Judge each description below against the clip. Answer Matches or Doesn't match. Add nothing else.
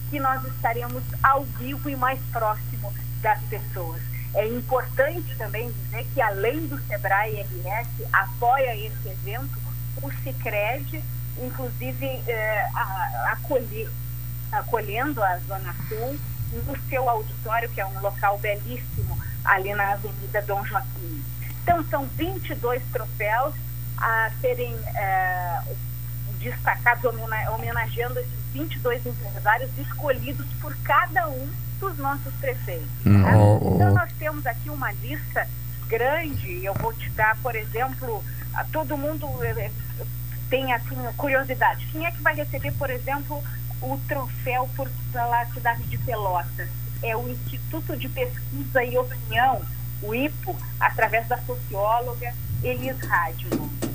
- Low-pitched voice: Matches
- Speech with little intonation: Matches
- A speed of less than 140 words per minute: Matches